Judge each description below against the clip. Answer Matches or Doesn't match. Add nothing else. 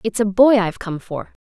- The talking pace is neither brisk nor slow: Doesn't match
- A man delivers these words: Doesn't match